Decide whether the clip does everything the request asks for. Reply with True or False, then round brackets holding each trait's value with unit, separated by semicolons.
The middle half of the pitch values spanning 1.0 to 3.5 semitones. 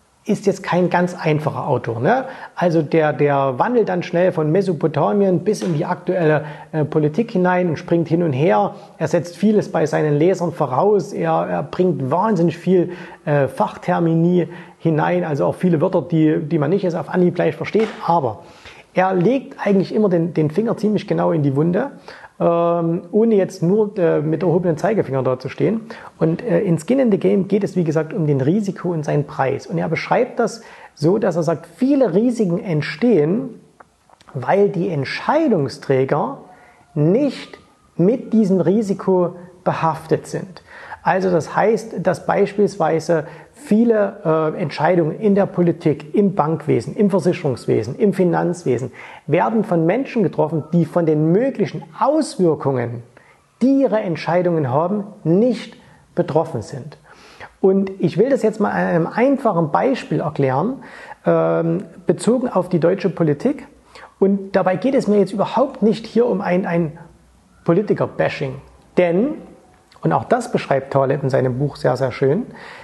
False (4.2 semitones)